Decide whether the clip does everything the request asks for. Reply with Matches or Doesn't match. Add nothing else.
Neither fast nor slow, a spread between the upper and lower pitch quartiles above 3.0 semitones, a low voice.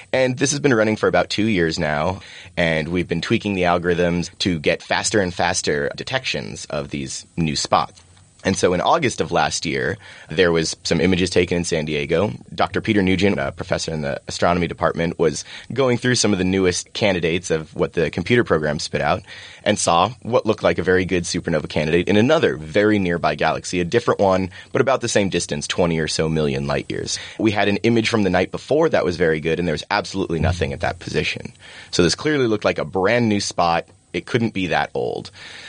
Doesn't match